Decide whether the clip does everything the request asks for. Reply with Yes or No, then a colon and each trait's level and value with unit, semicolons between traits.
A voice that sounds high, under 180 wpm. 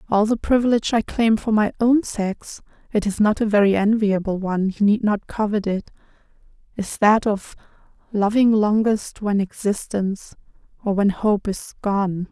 Yes: high, 210 Hz; average, 160 wpm